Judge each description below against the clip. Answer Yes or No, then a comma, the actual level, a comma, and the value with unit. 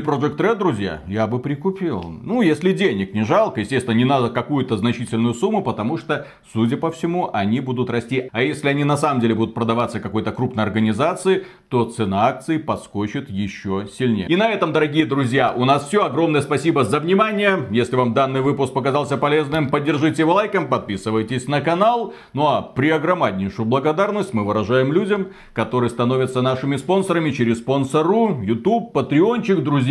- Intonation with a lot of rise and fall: Yes, wide, 6.0 semitones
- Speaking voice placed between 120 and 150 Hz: Yes, low, 135 Hz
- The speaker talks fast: Yes, fast, 170 wpm